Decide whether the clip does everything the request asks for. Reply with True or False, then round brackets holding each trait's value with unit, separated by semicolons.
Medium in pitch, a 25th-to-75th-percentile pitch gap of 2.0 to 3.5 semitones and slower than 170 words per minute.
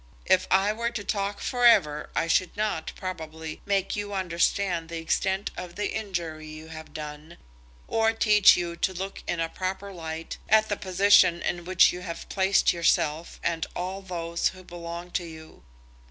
False (180 Hz; 3.2 semitones; 175 wpm)